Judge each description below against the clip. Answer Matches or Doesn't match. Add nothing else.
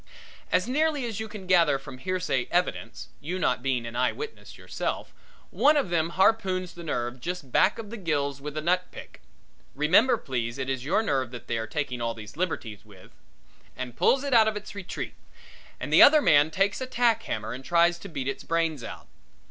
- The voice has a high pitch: Doesn't match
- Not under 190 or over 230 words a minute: Matches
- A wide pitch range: Matches